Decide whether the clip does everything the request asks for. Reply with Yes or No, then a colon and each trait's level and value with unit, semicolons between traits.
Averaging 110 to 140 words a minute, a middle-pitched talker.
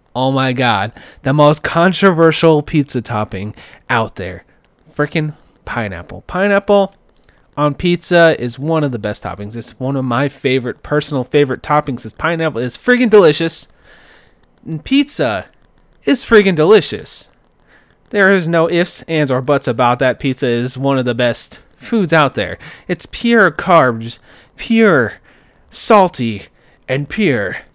Yes: slow, 135 wpm; medium, 150 Hz